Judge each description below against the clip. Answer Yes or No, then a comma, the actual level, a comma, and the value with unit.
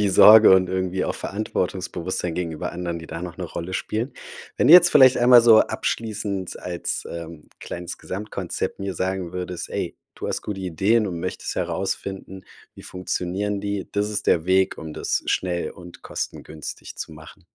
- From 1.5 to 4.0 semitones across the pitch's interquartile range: Yes, average, 2.8 semitones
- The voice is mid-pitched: No, very low, 95 Hz